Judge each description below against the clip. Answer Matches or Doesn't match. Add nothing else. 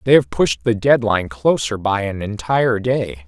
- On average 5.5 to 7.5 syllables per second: Doesn't match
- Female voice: Doesn't match